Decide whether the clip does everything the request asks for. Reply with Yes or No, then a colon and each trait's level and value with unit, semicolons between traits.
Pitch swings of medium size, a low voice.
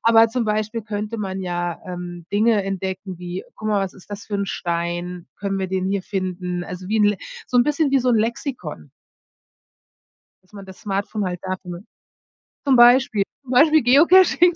No: average, 4.1 semitones; high, 200 Hz